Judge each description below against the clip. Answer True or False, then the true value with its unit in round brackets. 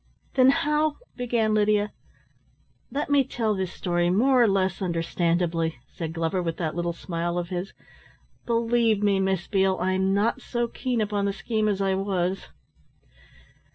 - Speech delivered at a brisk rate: False (155 wpm)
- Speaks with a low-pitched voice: False (195 Hz)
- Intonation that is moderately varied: True (4.6 semitones)